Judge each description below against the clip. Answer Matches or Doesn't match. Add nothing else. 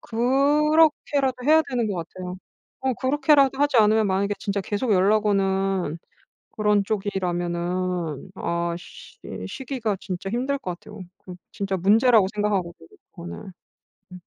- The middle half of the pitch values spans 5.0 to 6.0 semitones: Matches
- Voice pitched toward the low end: Doesn't match